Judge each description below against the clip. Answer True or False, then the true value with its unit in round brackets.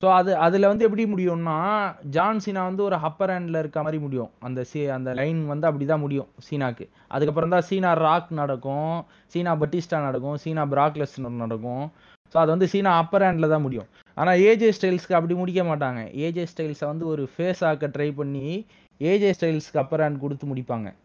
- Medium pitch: True (160 Hz)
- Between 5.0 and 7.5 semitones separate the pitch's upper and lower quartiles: False (4.1 semitones)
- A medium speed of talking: False (180 wpm)